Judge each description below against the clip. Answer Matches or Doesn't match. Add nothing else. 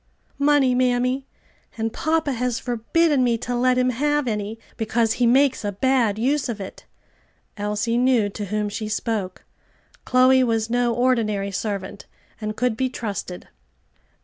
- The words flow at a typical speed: Matches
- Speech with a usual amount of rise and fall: Matches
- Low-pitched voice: Doesn't match